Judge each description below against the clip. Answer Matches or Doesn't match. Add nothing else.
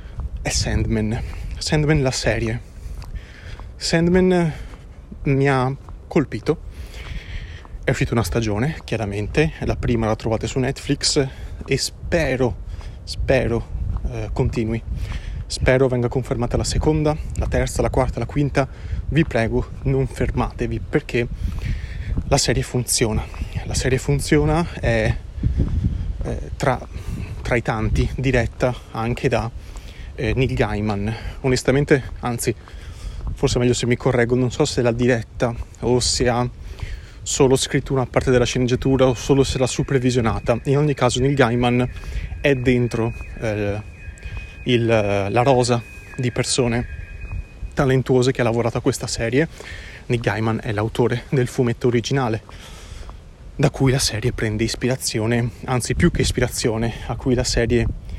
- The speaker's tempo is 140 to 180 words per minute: Doesn't match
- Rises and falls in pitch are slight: Doesn't match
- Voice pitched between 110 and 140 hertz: Matches